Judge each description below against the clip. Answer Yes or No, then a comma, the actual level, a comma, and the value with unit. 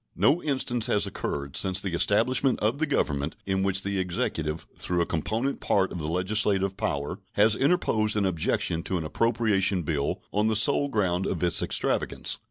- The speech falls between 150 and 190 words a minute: Yes, average, 180 wpm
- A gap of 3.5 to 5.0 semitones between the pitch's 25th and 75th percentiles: Yes, average, 4.1 semitones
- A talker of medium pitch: No, very low, 95 Hz